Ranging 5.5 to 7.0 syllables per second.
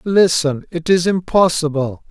No: 4.2 syllables/s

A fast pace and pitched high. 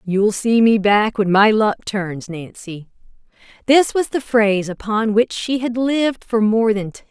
No: average, 195 wpm; high, 215 Hz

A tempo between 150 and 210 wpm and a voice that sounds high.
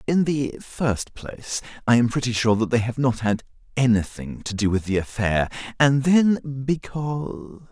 No: average, 170 wpm; low, 125 Hz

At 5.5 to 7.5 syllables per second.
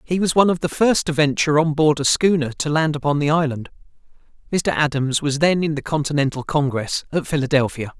Yes: 6.0 syllables/s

